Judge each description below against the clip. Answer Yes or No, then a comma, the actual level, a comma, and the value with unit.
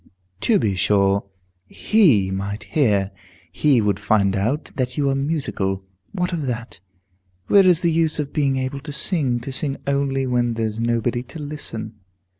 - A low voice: Yes, low, 130 Hz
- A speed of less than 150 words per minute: No, average, 165 wpm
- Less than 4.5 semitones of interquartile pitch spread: No, wide, 5.6 semitones